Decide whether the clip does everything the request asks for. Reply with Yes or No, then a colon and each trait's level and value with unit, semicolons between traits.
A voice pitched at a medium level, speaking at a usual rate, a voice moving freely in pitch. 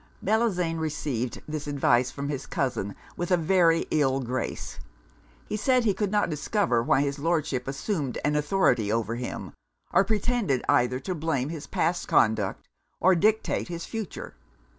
Yes: medium, 155 Hz; average, 160 wpm; wide, 6.4 semitones